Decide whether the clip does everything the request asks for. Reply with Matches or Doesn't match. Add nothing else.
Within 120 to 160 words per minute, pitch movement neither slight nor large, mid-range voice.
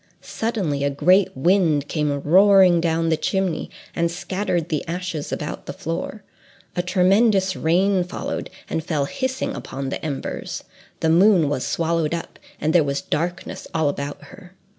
Matches